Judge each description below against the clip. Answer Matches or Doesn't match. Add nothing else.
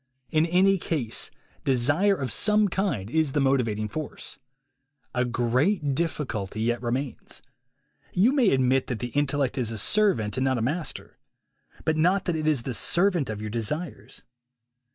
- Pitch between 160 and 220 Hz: Doesn't match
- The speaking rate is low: Doesn't match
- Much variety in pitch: Matches